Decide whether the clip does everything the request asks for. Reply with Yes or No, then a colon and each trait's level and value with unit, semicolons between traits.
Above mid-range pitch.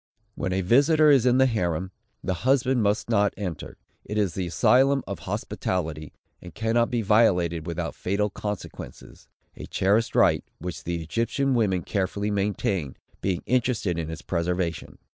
No: low, 100 Hz